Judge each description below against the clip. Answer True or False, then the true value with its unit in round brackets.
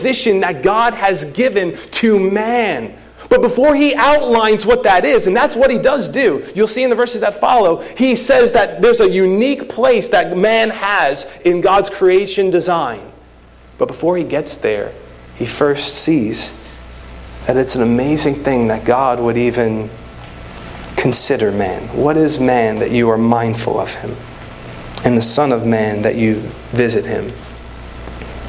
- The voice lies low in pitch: False (155 Hz)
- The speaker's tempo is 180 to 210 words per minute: False (160 wpm)